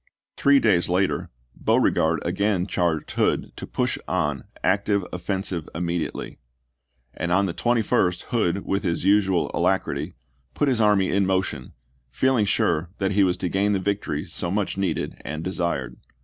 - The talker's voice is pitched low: Yes, very low, 95 Hz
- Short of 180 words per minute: Yes, average, 155 wpm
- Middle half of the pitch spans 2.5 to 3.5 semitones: Yes, average, 2.8 semitones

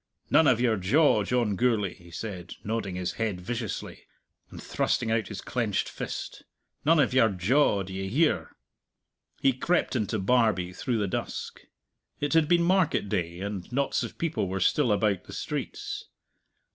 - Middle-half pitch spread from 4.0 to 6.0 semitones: Yes, average, 5.2 semitones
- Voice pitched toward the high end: No, low, 110 Hz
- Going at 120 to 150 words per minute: No, average, 160 wpm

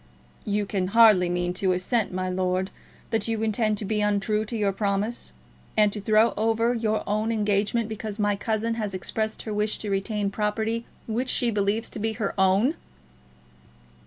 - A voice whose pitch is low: No, high, 210 Hz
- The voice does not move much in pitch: Yes, narrow, 2.0 semitones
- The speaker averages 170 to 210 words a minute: Yes, average, 175 wpm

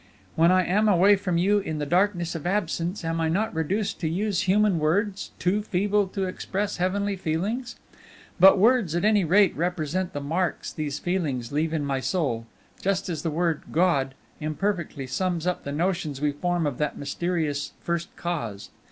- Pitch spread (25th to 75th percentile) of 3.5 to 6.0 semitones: Yes, average, 4.0 semitones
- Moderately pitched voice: Yes, medium, 175 Hz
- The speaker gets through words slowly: No, average, 180 wpm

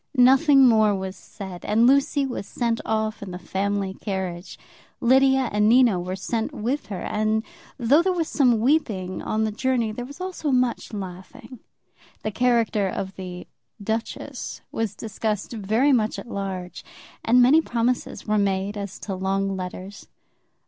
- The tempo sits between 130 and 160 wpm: Yes, average, 155 wpm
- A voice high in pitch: Yes, high, 220 Hz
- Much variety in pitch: No, average, 4.3 semitones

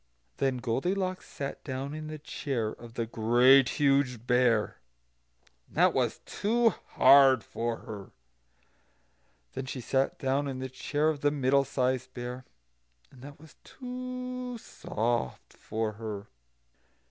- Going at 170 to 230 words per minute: No, slow, 135 wpm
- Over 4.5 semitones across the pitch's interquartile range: No, average, 3.5 semitones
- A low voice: Yes, low, 130 Hz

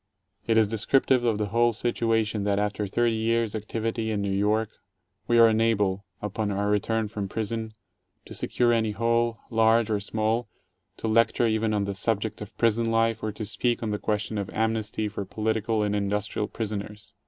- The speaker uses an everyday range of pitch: No, narrow, 1.6 semitones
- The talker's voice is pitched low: Yes, low, 110 Hz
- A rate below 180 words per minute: No, average, 190 wpm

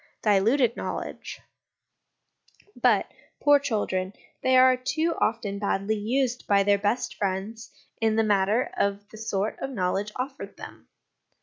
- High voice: Yes, high, 220 Hz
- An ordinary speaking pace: No, slow, 130 wpm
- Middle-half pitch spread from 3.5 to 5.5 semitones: Yes, average, 4.0 semitones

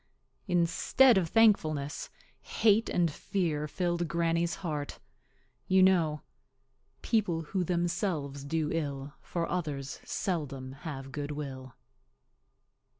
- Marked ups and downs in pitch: No, average, 3.7 semitones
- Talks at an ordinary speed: No, slow, 100 wpm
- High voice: No, medium, 165 Hz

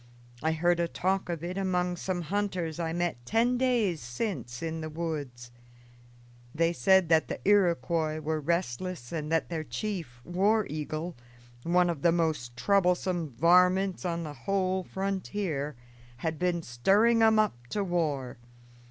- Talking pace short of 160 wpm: Yes, average, 150 wpm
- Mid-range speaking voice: Yes, medium, 170 Hz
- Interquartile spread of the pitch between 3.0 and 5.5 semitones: Yes, average, 3.5 semitones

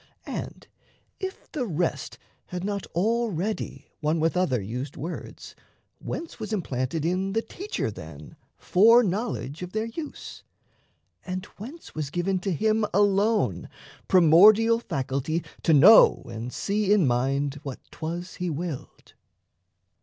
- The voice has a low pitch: No, medium, 180 Hz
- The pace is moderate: No, slow, 130 wpm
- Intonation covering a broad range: Yes, wide, 6.4 semitones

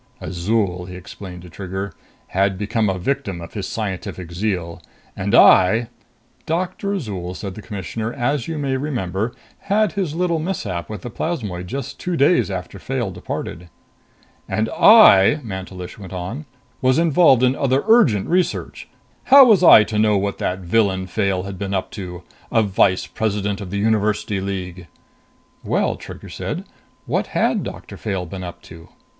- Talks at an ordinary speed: Yes, average, 160 wpm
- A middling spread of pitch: No, wide, 6.1 semitones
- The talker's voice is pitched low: Yes, low, 100 Hz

